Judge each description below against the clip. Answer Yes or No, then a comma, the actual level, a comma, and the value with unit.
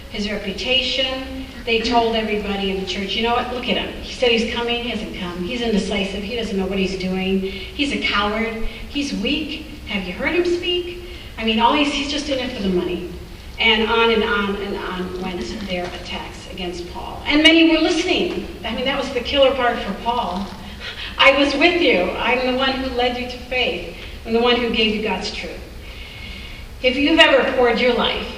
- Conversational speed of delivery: No, fast, 210 wpm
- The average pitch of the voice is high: Yes, high, 235 Hz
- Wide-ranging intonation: No, average, 4.7 semitones